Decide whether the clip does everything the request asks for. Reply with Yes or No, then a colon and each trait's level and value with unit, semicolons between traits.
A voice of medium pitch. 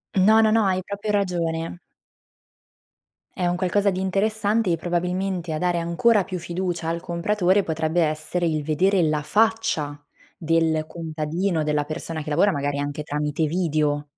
Yes: medium, 170 Hz